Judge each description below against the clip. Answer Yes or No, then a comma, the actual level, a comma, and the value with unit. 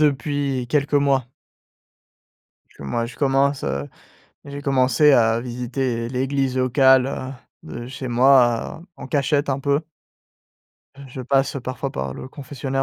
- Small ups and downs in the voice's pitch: Yes, narrow, 2.3 semitones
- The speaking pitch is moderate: No, low, 130 Hz